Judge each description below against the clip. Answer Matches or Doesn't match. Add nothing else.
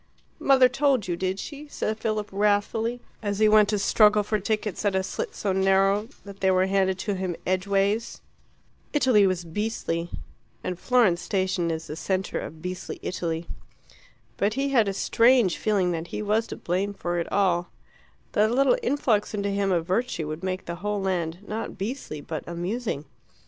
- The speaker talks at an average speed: Matches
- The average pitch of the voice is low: Doesn't match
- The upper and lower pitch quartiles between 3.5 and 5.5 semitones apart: Doesn't match